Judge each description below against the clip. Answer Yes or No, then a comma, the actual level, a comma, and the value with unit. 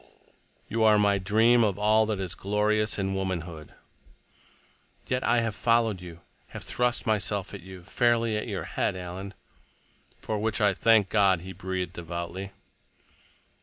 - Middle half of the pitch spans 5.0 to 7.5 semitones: No, average, 2.9 semitones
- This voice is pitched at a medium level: No, low, 100 Hz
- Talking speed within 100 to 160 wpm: Yes, average, 145 wpm